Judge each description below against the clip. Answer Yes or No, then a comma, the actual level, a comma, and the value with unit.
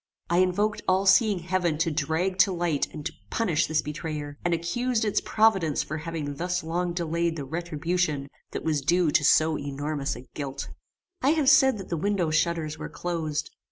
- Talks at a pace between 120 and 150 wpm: No, average, 185 wpm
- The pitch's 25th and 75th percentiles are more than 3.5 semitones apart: No, average, 3.2 semitones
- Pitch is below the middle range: No, medium, 170 Hz